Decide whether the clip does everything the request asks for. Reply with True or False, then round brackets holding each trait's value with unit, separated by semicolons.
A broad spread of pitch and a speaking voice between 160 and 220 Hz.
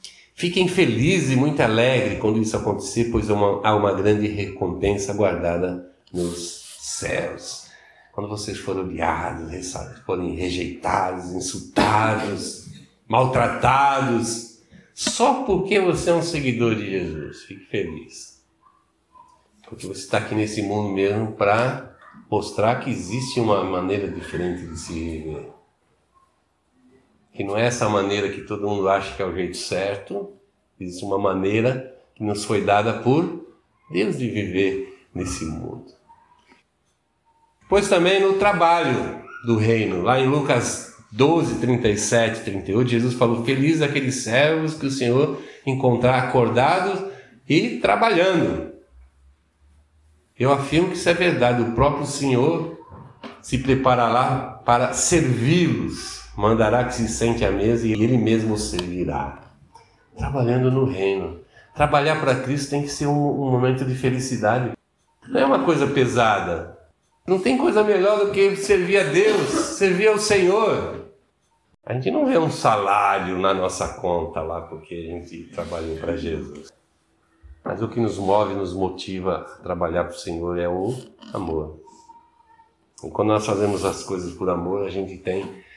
False (6.0 semitones; 115 Hz)